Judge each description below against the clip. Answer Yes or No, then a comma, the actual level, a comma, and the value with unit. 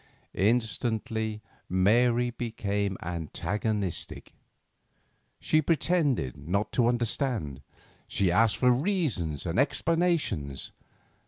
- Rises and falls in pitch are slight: No, average, 5.1 semitones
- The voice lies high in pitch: No, low, 110 Hz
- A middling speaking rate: No, slow, 80 wpm